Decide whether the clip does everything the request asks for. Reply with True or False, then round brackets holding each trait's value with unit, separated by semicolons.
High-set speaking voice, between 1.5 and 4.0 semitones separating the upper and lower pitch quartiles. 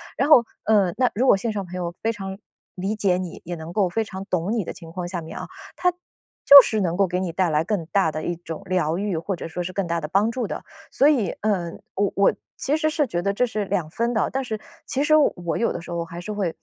False (195 Hz; 4.4 semitones)